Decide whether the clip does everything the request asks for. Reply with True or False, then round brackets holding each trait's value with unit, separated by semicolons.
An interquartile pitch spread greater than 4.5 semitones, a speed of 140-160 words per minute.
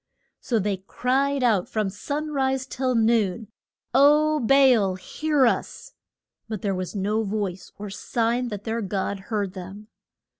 True (4.9 semitones; 150 wpm)